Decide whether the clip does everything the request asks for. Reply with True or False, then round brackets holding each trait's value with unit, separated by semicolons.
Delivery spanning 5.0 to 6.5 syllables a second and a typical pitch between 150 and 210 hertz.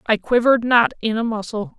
False (5.7 syllables/s; 225 Hz)